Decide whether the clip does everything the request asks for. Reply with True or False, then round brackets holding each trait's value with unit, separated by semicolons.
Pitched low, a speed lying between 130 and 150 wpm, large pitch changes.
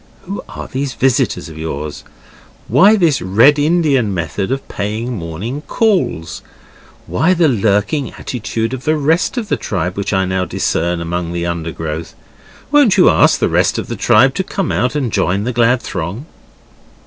False (115 Hz; 170 wpm; 8.6 semitones)